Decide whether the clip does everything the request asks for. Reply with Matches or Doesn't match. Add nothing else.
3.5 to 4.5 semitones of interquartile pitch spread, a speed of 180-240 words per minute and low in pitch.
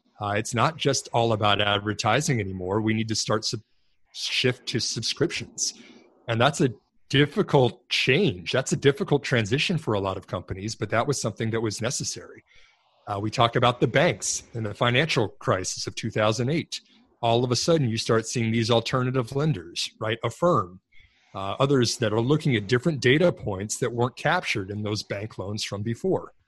Matches